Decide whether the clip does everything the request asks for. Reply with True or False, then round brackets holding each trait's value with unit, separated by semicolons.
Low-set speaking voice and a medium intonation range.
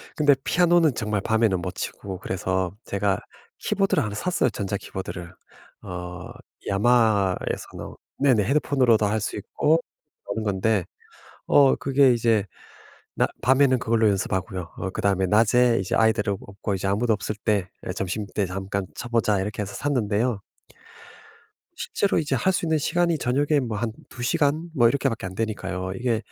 True (110 Hz; 4.9 semitones)